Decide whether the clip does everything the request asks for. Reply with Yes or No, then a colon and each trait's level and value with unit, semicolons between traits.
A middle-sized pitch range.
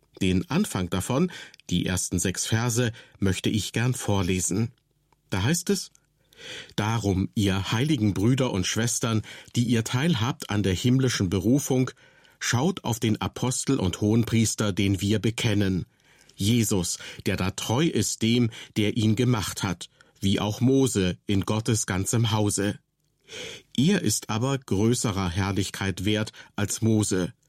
Yes: average, 4.0 semitones